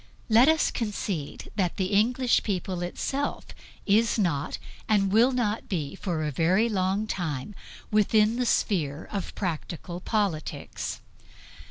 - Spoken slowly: Yes, slow, 130 wpm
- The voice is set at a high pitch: Yes, high, 200 Hz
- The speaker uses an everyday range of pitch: Yes, average, 4.0 semitones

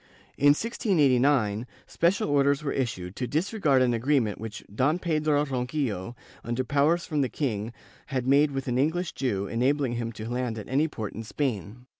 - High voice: No, low, 130 Hz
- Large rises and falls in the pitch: No, average, 4.1 semitones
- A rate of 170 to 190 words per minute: Yes, average, 180 wpm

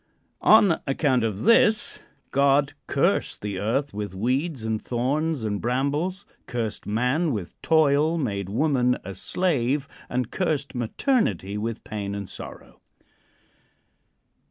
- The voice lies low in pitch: Yes, low, 125 Hz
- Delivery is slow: Yes, slow, 120 wpm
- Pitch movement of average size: No, wide, 5.9 semitones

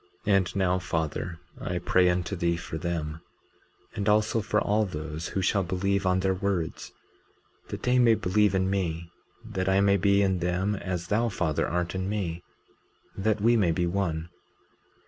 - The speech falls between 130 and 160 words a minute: No, average, 175 wpm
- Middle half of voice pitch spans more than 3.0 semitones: No, narrow, 2.6 semitones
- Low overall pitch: Yes, very low, 95 Hz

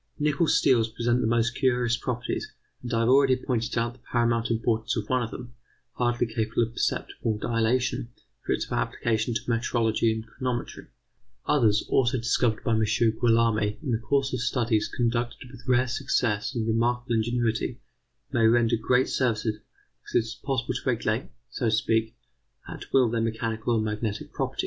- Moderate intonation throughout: No, narrow, 1.7 semitones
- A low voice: Yes, low, 115 Hz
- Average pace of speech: Yes, average, 170 wpm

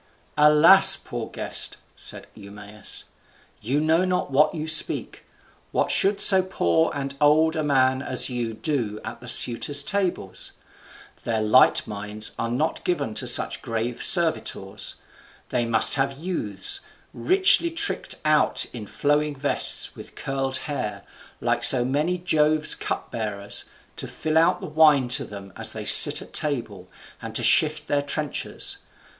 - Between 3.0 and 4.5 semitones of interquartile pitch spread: No, wide, 5.5 semitones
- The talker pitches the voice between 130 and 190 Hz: Yes, medium, 140 Hz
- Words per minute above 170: No, average, 150 wpm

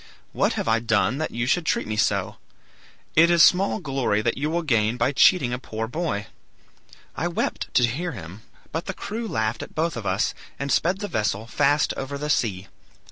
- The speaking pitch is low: Yes, low, 130 Hz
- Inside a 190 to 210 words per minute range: Yes, average, 195 wpm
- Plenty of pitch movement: Yes, wide, 6.3 semitones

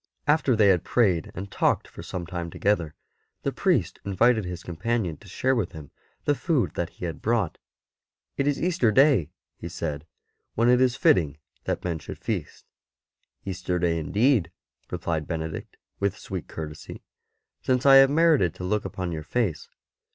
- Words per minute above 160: Yes, average, 180 wpm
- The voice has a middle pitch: No, very low, 95 Hz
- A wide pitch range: Yes, wide, 6.6 semitones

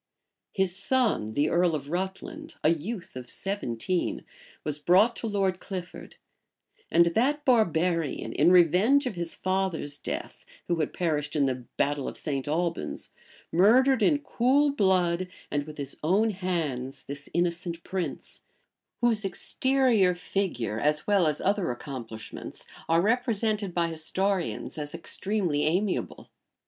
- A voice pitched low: No, medium, 180 Hz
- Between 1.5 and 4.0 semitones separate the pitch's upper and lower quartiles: No, average, 5.3 semitones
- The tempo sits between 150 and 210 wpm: No, slow, 135 wpm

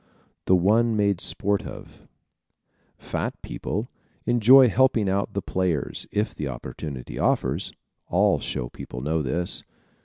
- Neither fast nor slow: No, slow, 130 wpm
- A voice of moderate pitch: No, low, 100 Hz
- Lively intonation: Yes, wide, 5.9 semitones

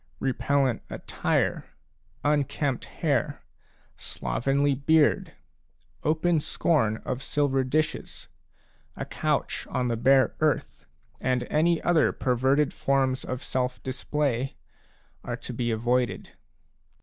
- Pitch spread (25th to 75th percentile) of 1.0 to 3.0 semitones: Yes, average, 2.7 semitones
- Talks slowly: Yes, slow, 105 wpm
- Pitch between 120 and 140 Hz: Yes, low, 135 Hz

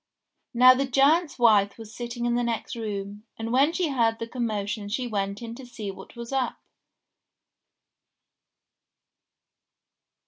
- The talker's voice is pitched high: Yes, high, 235 Hz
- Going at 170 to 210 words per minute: No, average, 140 wpm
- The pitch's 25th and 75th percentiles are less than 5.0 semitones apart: Yes, average, 3.2 semitones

